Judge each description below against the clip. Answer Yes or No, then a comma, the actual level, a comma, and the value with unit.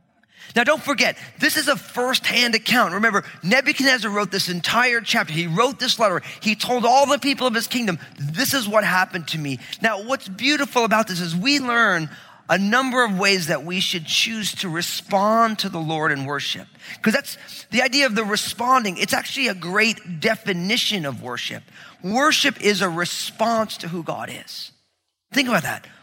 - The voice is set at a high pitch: Yes, high, 215 Hz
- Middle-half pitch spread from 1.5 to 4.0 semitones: No, wide, 5.5 semitones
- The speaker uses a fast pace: No, average, 185 wpm